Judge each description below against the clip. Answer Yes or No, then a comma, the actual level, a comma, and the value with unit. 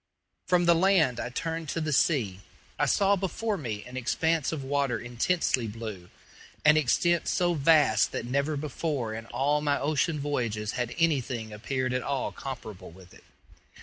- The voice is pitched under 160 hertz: Yes, medium, 140 Hz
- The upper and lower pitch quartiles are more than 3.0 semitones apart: Yes, wide, 5.5 semitones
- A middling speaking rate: Yes, average, 165 wpm